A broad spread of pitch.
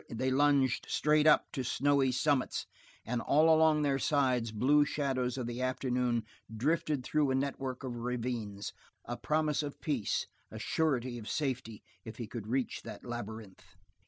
No: average, 3.4 semitones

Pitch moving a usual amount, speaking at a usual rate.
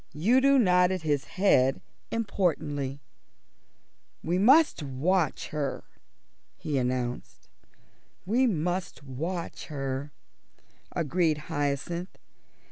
No: average, 5.0 semitones; slow, 80 wpm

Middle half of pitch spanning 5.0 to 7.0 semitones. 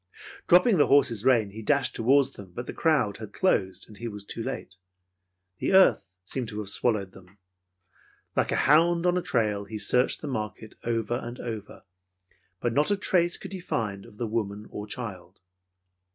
Yes: wide, 5.4 semitones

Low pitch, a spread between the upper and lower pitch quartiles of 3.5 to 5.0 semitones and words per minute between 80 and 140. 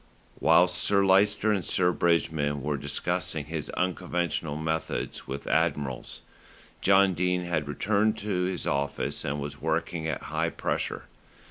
Yes: very low, 85 Hz; average, 4.4 semitones; slow, 135 wpm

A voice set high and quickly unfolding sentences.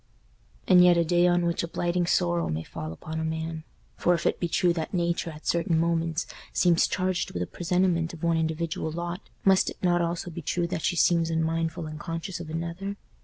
No: medium, 170 Hz; fast, 210 wpm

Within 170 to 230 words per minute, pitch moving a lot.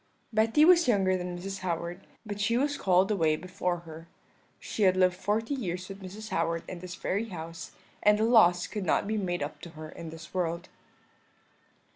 No: average, 190 wpm; average, 3.4 semitones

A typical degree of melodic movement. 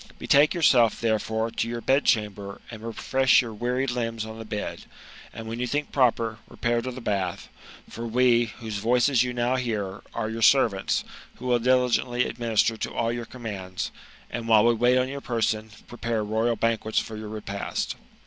No: narrow, 2.1 semitones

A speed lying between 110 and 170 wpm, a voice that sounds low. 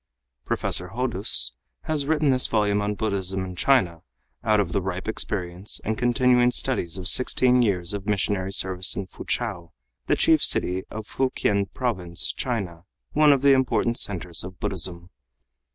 Yes: average, 150 wpm; low, 100 Hz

